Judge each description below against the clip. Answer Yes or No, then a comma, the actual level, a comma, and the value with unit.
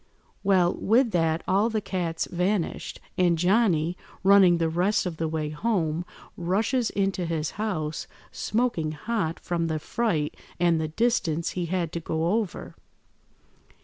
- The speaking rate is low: No, average, 145 wpm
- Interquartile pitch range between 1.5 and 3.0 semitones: No, average, 3.9 semitones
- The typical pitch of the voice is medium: Yes, medium, 175 Hz